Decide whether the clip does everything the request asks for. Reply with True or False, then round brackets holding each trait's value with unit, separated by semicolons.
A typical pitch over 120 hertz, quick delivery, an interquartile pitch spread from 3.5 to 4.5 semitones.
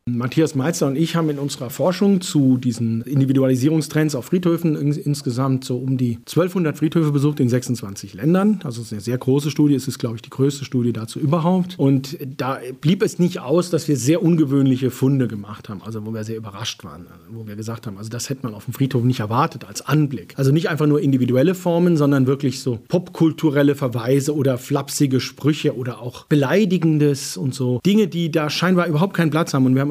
True (140 Hz; 210 wpm; 4.1 semitones)